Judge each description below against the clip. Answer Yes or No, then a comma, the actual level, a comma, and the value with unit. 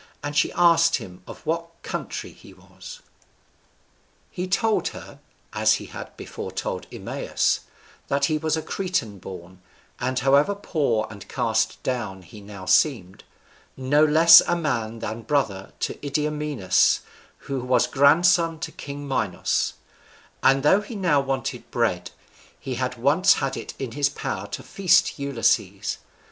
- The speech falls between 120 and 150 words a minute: Yes, average, 145 wpm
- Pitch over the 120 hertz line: Yes, medium, 140 Hz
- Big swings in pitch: Yes, wide, 6.1 semitones